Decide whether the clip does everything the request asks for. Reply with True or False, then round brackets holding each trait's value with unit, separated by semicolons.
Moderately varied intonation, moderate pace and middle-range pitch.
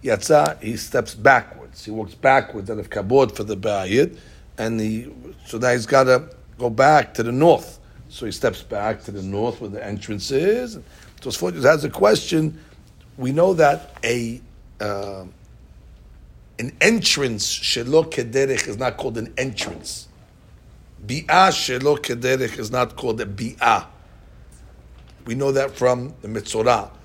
False (4.4 semitones; 150 wpm; 115 Hz)